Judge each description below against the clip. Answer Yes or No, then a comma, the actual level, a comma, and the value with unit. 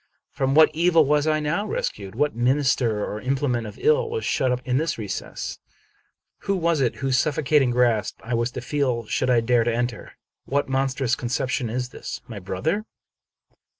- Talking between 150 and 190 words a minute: Yes, average, 185 wpm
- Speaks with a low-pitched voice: Yes, low, 130 Hz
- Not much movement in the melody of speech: No, average, 3.8 semitones